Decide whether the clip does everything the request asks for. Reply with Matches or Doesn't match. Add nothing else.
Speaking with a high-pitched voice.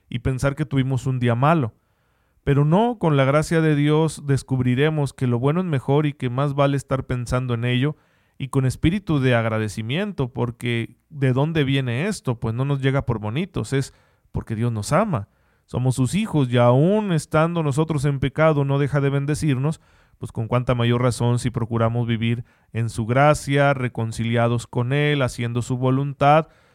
Doesn't match